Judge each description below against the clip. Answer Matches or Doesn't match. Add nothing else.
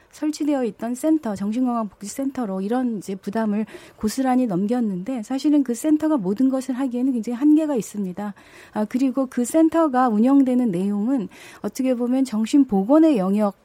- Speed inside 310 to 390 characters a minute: Matches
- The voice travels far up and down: Doesn't match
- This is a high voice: Matches